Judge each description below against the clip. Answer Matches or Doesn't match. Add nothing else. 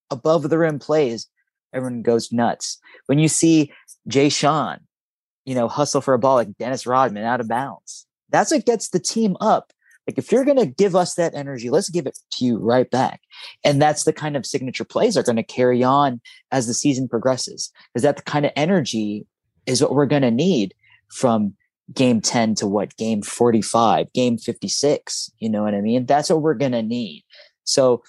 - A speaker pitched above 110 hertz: Matches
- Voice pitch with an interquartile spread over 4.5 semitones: Matches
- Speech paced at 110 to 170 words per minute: Doesn't match